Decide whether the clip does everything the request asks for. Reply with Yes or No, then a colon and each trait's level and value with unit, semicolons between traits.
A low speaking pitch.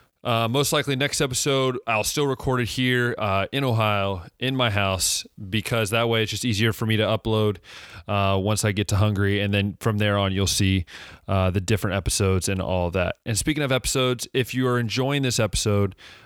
Yes: low, 110 Hz